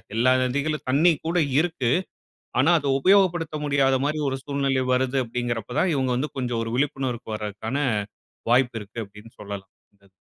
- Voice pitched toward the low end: Yes, low, 130 Hz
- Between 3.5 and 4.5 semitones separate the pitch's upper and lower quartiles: Yes, average, 4.0 semitones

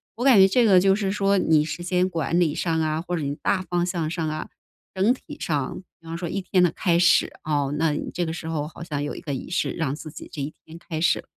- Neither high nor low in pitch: Yes, medium, 170 Hz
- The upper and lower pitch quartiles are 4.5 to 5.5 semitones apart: No, average, 3.0 semitones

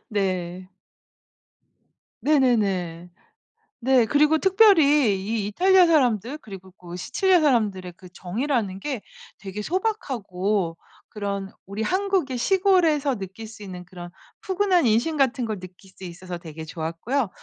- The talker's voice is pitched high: Yes, high, 215 Hz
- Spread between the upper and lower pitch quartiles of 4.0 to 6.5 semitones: No, wide, 8.1 semitones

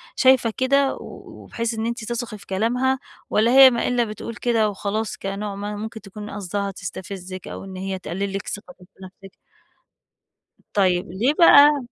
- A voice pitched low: No, high, 210 Hz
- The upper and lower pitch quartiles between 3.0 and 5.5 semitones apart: Yes, average, 3.5 semitones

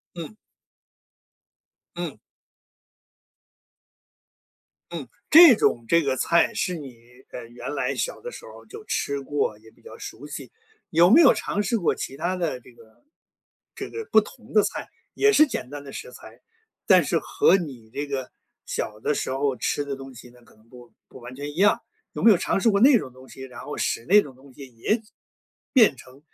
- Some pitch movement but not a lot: No, wide, 8.3 semitones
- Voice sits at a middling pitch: Yes, medium, 145 Hz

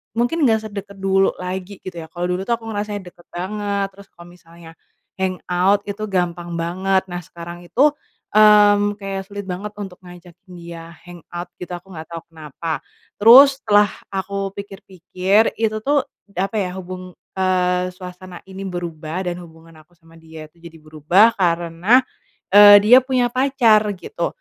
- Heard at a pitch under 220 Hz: Yes, medium, 185 Hz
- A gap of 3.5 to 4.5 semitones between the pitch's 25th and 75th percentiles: No, average, 3.0 semitones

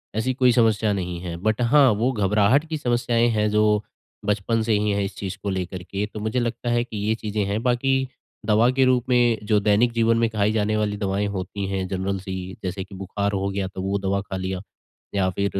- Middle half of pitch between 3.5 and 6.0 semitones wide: No, average, 3.1 semitones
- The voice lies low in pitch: Yes, low, 105 Hz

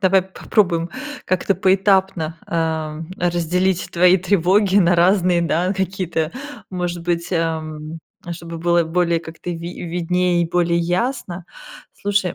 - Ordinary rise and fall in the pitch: No, narrow, 1.9 semitones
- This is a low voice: No, medium, 175 Hz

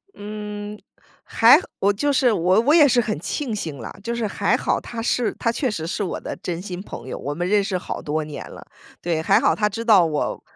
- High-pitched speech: Yes, high, 205 Hz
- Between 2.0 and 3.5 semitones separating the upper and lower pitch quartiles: No, average, 4.8 semitones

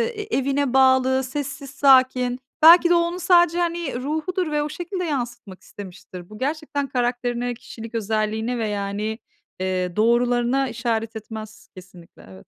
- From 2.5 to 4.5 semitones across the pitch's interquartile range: No, average, 5.0 semitones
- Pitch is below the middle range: No, high, 245 Hz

